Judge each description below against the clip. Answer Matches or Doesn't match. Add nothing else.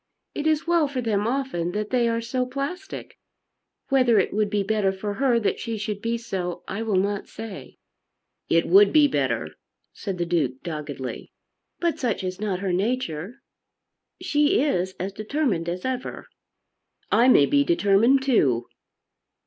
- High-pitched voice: Matches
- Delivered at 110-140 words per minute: Doesn't match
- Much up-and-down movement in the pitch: Matches